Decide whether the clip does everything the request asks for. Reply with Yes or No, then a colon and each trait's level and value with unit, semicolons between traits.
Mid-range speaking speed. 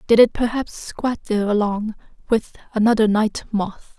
Yes: average, 150 wpm